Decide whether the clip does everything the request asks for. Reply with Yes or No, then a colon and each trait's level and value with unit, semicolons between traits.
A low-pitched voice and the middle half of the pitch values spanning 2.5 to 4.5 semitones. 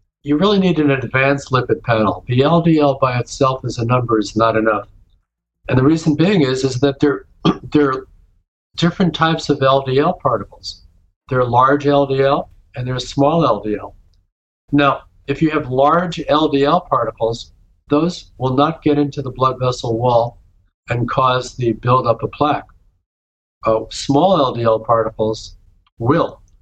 No: low, 130 Hz; average, 4.9 semitones